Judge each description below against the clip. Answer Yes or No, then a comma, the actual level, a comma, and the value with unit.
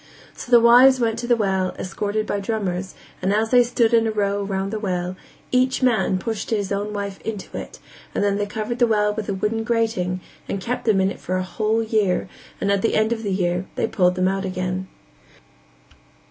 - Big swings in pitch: No, average, 2.9 semitones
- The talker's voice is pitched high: Yes, high, 205 Hz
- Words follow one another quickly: Yes, fast, 215 wpm